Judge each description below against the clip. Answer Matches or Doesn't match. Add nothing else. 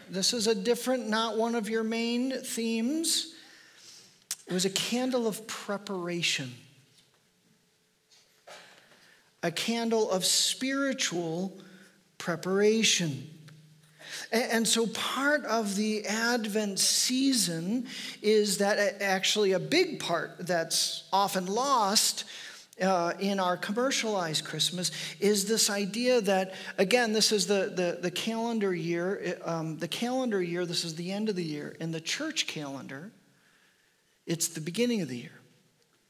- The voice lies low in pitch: Doesn't match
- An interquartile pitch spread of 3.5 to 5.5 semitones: Matches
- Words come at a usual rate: Doesn't match